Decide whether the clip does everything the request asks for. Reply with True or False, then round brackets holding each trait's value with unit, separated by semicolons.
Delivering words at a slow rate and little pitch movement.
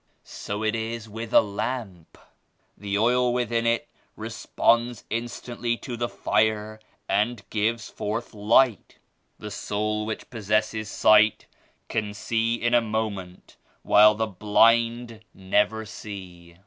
True (125 wpm; 2.0 semitones)